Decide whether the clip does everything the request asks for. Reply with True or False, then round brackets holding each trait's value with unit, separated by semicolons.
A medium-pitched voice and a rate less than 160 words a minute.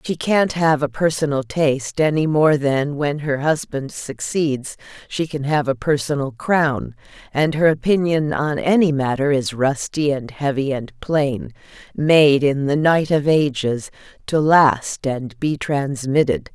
True (145 Hz; 150 wpm)